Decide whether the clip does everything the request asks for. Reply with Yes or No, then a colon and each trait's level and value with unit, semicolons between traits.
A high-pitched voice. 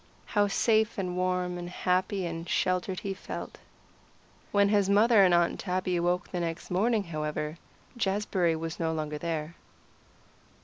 No: medium, 180 Hz